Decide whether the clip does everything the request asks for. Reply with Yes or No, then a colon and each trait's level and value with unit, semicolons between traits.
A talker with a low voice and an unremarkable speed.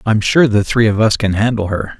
No: low, 110 Hz; fast, 270 wpm